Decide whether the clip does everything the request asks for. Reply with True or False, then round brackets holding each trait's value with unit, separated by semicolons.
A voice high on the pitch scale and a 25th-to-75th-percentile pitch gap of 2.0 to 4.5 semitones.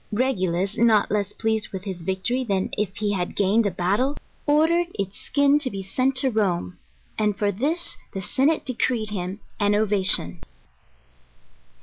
False (210 Hz; 5.0 semitones)